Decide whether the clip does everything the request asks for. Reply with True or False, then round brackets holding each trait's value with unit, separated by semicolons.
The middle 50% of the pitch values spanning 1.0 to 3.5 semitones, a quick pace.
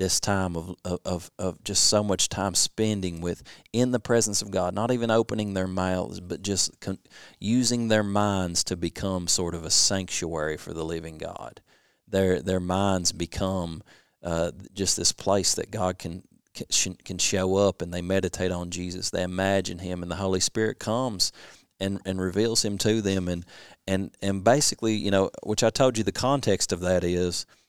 False (2.7 semitones; 190 wpm)